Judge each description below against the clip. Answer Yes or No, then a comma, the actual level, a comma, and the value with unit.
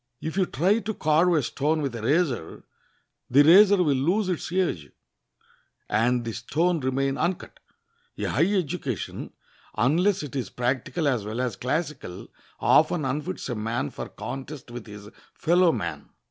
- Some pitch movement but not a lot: No, wide, 6.1 semitones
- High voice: No, medium, 145 Hz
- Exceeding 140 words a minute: Yes, average, 155 wpm